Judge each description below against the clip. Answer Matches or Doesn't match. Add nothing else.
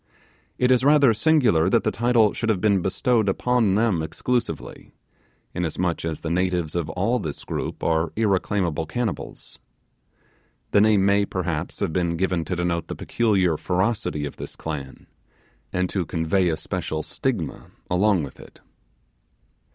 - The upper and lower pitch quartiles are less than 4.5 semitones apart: Doesn't match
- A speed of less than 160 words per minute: Matches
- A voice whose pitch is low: Matches